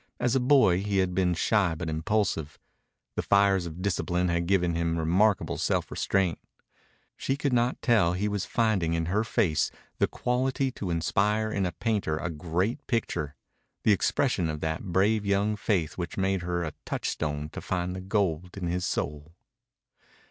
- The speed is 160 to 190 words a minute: Yes, average, 170 wpm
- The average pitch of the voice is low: Yes, very low, 95 Hz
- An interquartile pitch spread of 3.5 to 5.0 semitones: Yes, average, 3.8 semitones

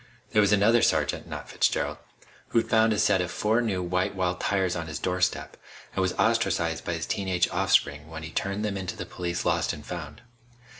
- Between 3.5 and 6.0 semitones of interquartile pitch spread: No, average, 3.1 semitones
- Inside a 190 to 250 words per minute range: Yes, fast, 205 wpm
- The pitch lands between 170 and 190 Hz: No, very low, 90 Hz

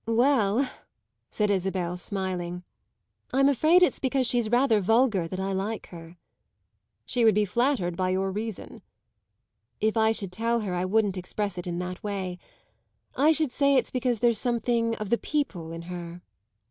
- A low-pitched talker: No, high, 210 Hz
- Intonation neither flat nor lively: Yes, average, 4.7 semitones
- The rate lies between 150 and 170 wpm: Yes, average, 165 wpm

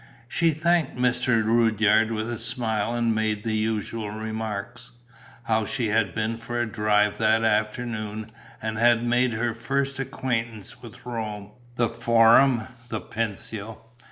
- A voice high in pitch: No, low, 115 Hz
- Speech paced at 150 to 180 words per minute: No, average, 140 wpm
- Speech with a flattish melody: Yes, narrow, 1.8 semitones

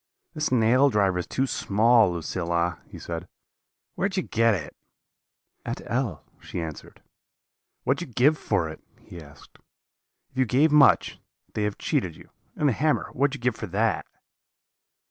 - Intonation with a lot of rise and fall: Yes, wide, 7.2 semitones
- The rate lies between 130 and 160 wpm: No, average, 175 wpm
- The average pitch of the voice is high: No, low, 115 Hz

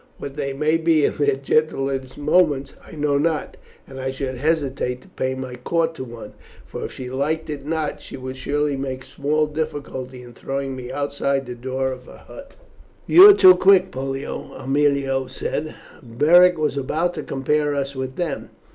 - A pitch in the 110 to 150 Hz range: Yes, medium, 140 Hz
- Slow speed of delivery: No, average, 180 wpm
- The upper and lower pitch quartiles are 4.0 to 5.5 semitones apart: No, average, 2.8 semitones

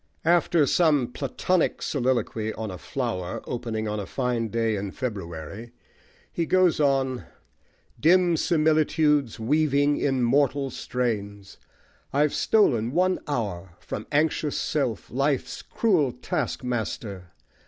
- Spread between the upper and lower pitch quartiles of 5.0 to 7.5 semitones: Yes, wide, 5.4 semitones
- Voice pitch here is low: Yes, low, 130 Hz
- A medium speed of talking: No, slow, 110 wpm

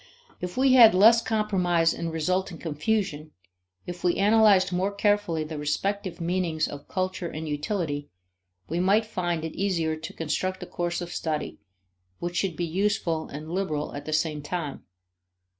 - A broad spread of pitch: No, average, 3.7 semitones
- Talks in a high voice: No, medium, 175 Hz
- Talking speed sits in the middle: Yes, average, 160 wpm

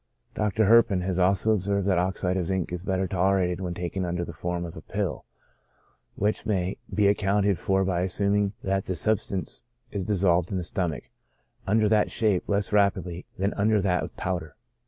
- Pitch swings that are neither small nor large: No, narrow, 2.2 semitones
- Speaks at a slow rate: No, average, 180 wpm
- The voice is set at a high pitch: No, very low, 95 Hz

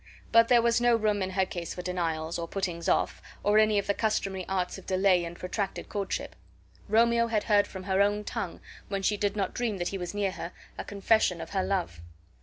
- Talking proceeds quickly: Yes, fast, 220 wpm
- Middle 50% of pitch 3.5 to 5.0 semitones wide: No, narrow, 2.6 semitones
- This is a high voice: Yes, high, 195 Hz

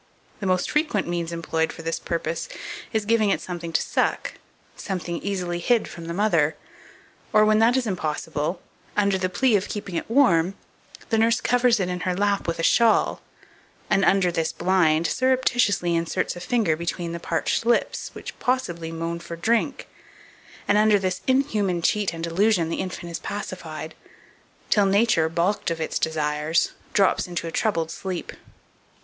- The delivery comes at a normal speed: Yes, average, 165 wpm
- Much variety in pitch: No, average, 4.2 semitones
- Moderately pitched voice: Yes, medium, 180 Hz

